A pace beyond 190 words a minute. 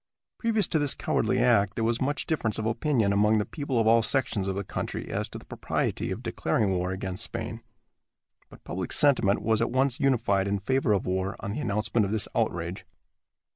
Yes: fast, 205 wpm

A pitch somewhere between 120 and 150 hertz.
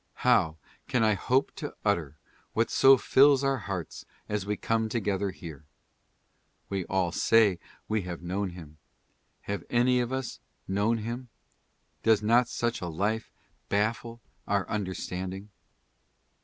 No: low, 105 Hz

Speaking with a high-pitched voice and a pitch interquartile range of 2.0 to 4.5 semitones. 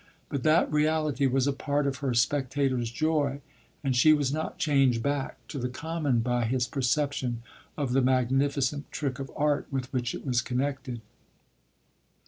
No: low, 135 Hz; narrow, 2.5 semitones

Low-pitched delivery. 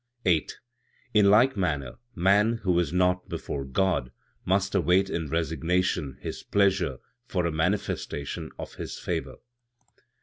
Yes: very low, 90 Hz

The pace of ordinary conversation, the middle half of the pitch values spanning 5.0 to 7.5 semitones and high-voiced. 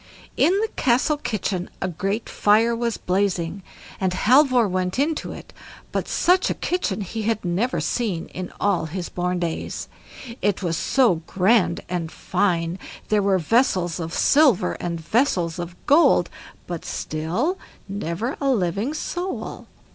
Yes: average, 145 wpm; wide, 5.5 semitones; high, 195 Hz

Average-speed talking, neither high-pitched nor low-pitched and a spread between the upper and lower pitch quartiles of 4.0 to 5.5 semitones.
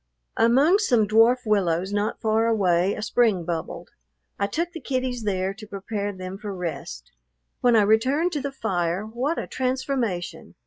No: average, 165 wpm; high, 215 Hz; average, 4.9 semitones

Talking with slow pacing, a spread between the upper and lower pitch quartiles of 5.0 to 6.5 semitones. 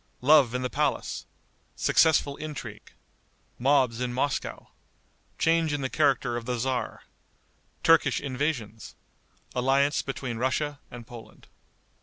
No: slow, 115 wpm; average, 3.0 semitones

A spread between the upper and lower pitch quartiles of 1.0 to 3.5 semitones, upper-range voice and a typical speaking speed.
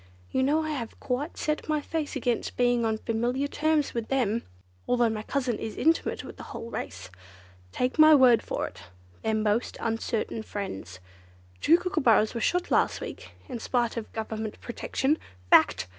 No: average, 4.6 semitones; high, 240 Hz; average, 170 wpm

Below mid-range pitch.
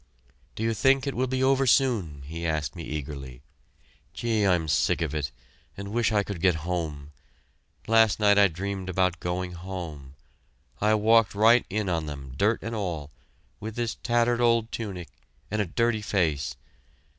Yes: low, 100 Hz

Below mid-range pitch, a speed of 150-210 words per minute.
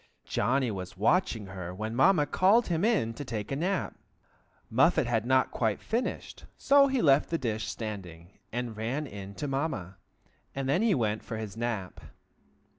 Yes: low, 120 Hz; average, 170 wpm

